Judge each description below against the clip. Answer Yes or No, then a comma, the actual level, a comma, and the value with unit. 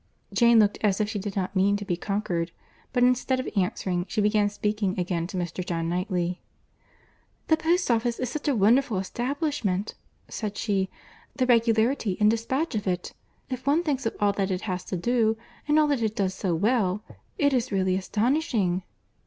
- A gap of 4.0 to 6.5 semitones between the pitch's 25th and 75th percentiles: Yes, average, 4.6 semitones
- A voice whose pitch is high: Yes, high, 210 Hz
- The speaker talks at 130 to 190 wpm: Yes, average, 180 wpm